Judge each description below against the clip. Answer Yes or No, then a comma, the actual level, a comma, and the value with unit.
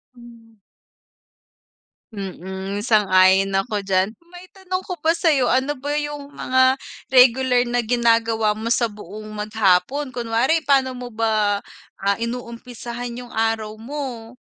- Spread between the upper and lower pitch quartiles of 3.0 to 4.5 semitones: Yes, average, 3.4 semitones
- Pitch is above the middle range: Yes, high, 235 Hz